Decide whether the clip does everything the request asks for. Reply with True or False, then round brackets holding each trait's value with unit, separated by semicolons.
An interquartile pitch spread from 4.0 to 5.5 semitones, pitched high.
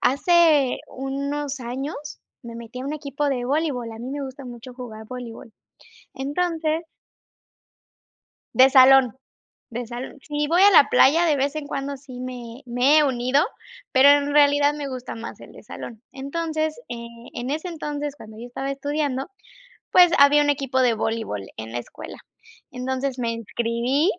False (3.0 semitones; 270 Hz)